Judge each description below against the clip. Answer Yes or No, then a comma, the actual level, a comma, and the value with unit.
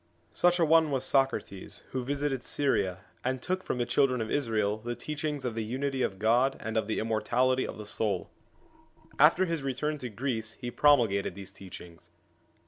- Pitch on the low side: Yes, low, 125 Hz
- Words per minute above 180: Yes, average, 190 wpm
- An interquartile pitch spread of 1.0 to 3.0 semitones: No, average, 4.4 semitones